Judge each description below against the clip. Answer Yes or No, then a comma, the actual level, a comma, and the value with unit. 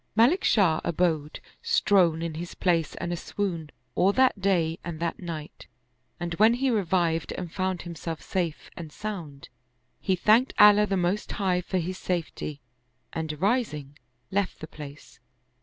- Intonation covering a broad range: No, average, 3.6 semitones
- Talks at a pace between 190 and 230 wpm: No, average, 150 wpm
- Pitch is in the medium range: Yes, medium, 175 Hz